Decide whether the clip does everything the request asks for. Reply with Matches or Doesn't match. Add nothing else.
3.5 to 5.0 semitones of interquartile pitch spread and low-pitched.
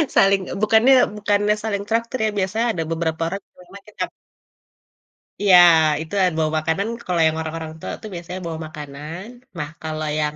Doesn't match